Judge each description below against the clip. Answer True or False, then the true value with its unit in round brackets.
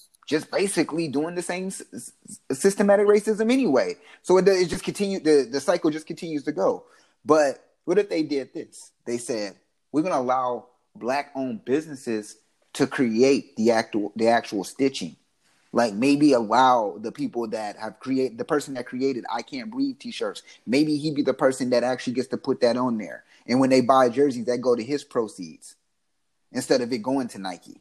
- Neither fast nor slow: True (185 wpm)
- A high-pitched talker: False (140 Hz)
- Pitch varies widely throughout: True (6.7 semitones)